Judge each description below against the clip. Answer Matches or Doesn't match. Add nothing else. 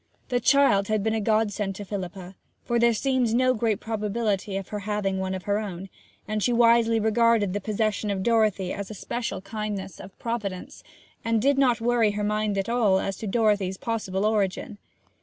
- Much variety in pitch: Doesn't match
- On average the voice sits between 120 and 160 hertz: Doesn't match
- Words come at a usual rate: Matches